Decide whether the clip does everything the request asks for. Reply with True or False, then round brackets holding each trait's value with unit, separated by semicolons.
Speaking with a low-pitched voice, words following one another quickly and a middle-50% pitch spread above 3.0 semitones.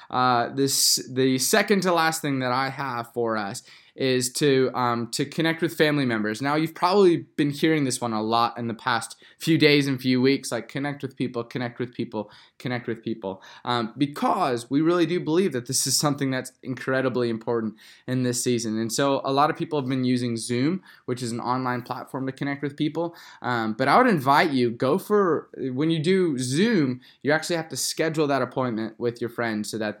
True (130 Hz; 210 wpm; 3.7 semitones)